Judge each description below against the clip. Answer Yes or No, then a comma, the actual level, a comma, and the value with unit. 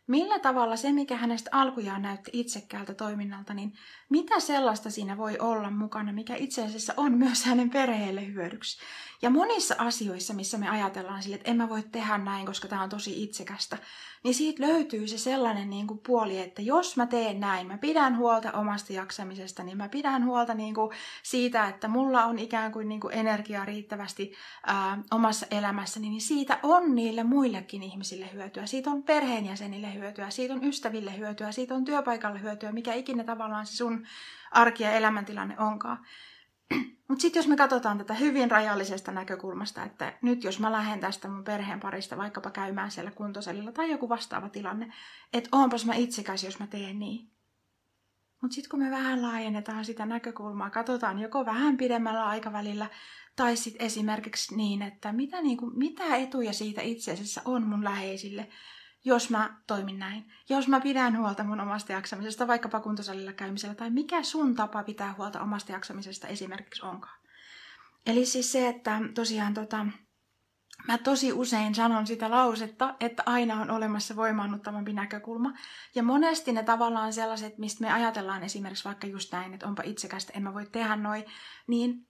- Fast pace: Yes, fast, 165 wpm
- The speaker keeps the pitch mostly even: No, average, 3.2 semitones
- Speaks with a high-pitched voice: Yes, high, 220 Hz